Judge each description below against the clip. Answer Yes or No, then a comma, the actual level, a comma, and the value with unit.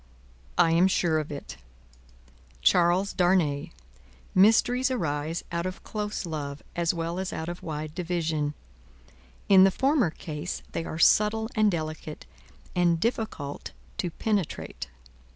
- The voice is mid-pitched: Yes, medium, 175 Hz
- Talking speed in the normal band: No, slow, 130 wpm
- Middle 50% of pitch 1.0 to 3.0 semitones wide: No, average, 3.8 semitones